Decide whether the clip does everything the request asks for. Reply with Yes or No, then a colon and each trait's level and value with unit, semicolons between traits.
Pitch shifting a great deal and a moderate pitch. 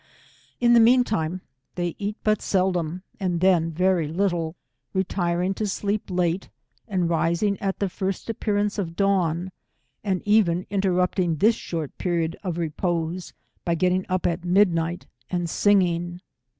No: average, 2.7 semitones; medium, 180 Hz